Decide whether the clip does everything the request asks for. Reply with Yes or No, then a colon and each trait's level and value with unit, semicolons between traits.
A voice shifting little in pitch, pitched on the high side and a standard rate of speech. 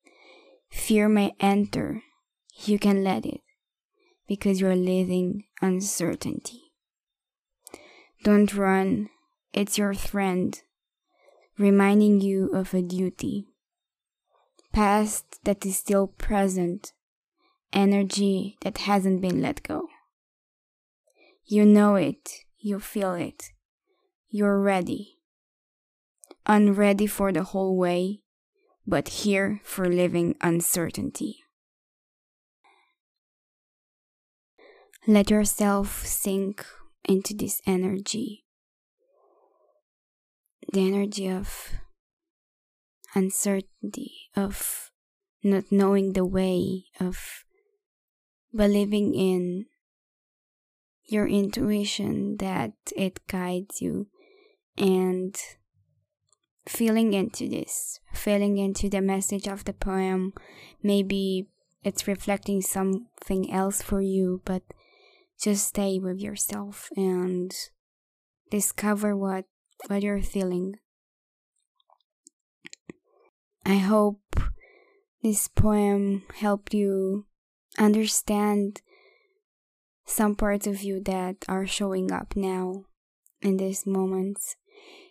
No: narrow, 2.1 semitones; high, 200 Hz; slow, 85 wpm